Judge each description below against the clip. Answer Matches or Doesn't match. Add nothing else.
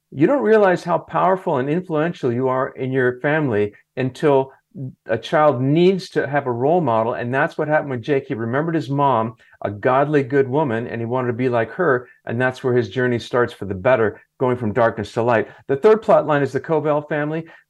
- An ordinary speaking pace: Doesn't match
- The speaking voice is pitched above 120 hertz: Matches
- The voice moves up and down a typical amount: Matches